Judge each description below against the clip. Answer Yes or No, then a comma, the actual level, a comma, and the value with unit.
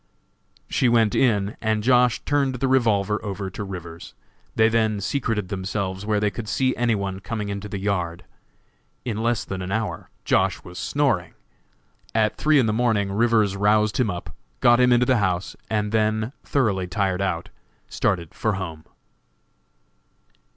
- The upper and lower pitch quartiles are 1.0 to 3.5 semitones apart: Yes, average, 3.2 semitones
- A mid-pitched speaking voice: No, low, 105 Hz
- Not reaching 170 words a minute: Yes, average, 160 wpm